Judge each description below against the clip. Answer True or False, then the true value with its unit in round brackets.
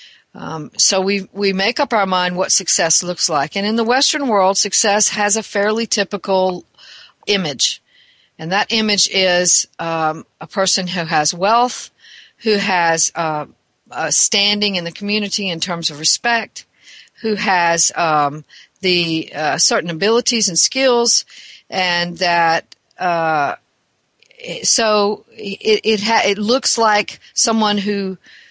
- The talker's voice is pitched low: False (200 Hz)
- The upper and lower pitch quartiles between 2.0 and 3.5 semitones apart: False (4.0 semitones)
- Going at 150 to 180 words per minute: False (140 wpm)